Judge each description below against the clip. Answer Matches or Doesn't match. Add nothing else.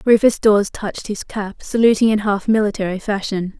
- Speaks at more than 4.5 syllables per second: Matches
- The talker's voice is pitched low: Doesn't match